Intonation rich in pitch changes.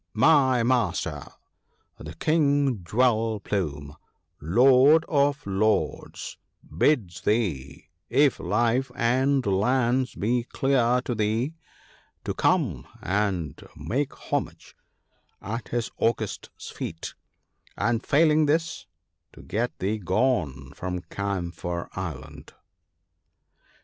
Yes: wide, 5.9 semitones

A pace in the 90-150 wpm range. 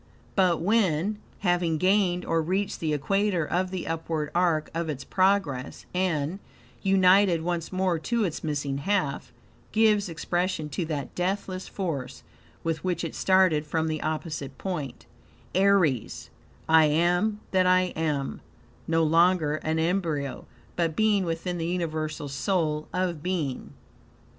Yes: slow, 135 wpm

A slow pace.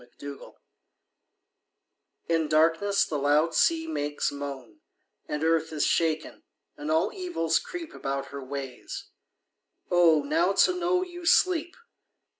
Yes: slow, 125 wpm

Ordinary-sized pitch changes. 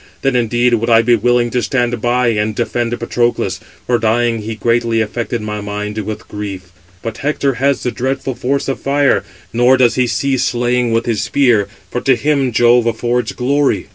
No: narrow, 1.8 semitones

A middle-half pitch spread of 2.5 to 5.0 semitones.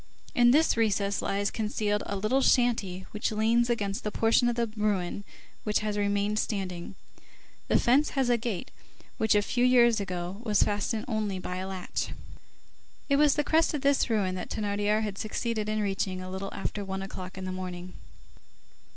Yes: average, 3.3 semitones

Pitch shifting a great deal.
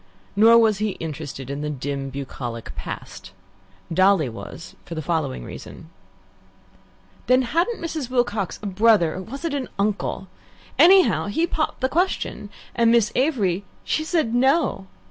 Yes: wide, 8.3 semitones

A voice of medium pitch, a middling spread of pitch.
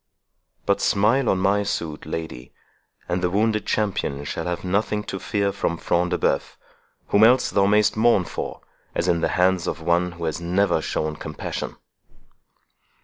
No: very low, 95 Hz; average, 3.3 semitones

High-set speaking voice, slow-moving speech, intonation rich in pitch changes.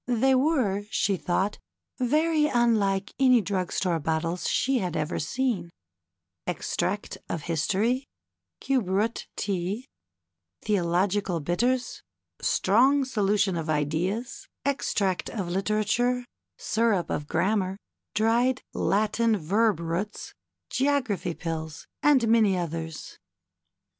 Yes: high, 205 Hz; slow, 105 wpm; wide, 5.7 semitones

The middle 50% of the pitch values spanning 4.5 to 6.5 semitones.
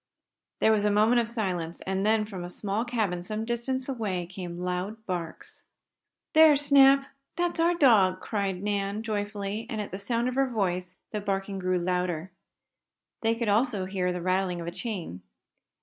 No: average, 4.1 semitones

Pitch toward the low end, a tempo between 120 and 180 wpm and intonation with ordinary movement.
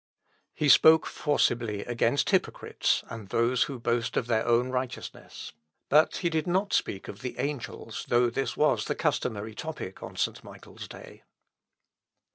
Yes: low, 120 Hz; average, 150 wpm; average, 4.4 semitones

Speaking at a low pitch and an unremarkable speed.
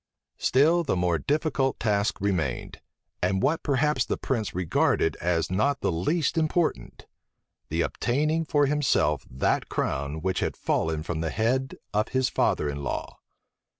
Yes: low, 110 Hz; average, 150 wpm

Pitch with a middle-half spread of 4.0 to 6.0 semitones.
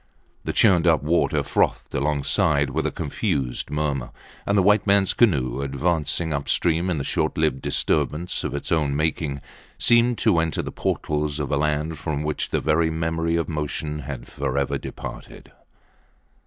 No: average, 2.9 semitones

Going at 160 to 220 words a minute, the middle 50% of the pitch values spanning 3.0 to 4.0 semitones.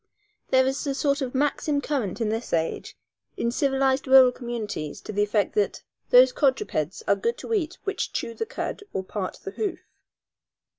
No: average, 180 wpm; average, 5.1 semitones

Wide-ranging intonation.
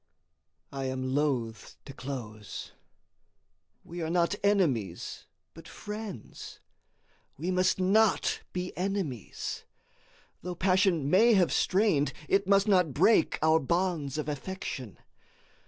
Yes: wide, 5.8 semitones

